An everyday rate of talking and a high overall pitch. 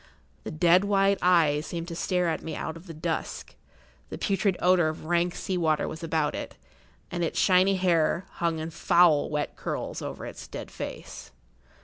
No: average, 180 wpm; medium, 170 Hz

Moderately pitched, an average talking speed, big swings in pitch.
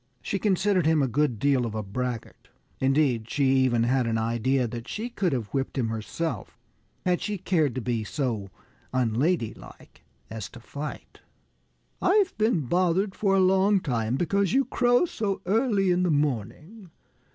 Yes: medium, 145 Hz; average, 165 wpm; wide, 8.3 semitones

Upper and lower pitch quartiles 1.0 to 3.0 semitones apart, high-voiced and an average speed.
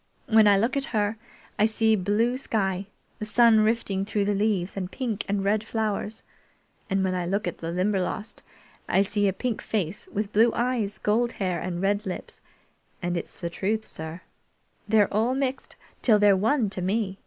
Yes: narrow, 2.5 semitones; high, 205 Hz; average, 180 wpm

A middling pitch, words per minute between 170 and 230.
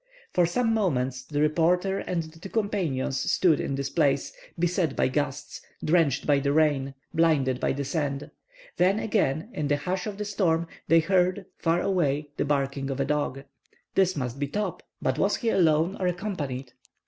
Yes: medium, 160 Hz; average, 185 wpm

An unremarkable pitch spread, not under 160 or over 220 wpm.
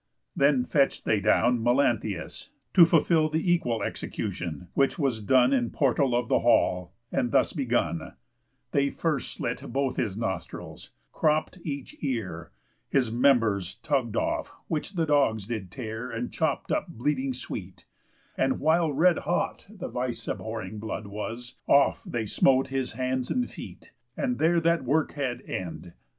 No: average, 4.4 semitones; average, 150 wpm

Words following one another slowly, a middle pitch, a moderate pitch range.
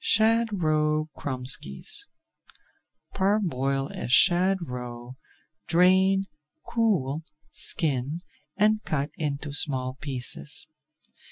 No: slow, 80 wpm; medium, 155 Hz; wide, 6.3 semitones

